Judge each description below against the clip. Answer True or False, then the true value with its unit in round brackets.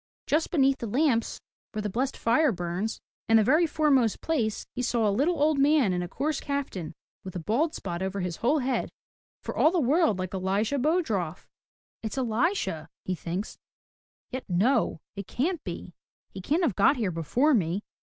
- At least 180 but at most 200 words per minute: True (190 wpm)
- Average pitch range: False (7.3 semitones)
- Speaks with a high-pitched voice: True (235 Hz)